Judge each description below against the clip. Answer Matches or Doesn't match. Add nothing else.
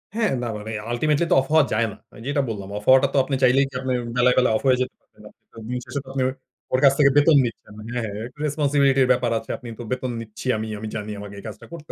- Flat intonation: Doesn't match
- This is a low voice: Matches